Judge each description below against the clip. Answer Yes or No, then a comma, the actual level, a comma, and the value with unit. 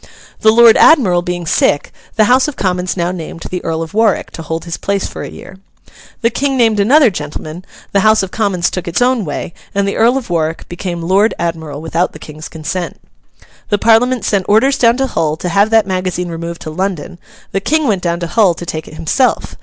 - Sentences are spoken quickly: Yes, fast, 215 wpm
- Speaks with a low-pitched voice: No, medium, 185 Hz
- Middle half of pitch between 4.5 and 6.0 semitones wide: Yes, average, 4.8 semitones